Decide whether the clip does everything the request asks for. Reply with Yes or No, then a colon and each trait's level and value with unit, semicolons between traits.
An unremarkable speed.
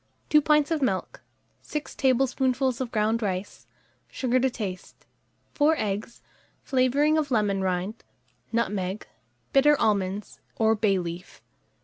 No: slow, 120 wpm